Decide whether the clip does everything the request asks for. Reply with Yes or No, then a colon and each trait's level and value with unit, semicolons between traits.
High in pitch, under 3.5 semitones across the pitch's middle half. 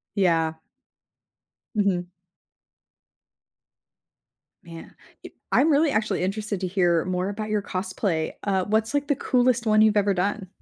Yes: high, 200 Hz; average, 3.1 semitones